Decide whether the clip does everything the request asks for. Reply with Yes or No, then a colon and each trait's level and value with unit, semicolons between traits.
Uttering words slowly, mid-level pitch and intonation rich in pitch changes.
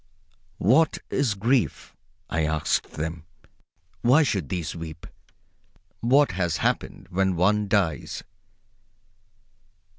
No: slow, 100 wpm; very low, 95 Hz; wide, 6.2 semitones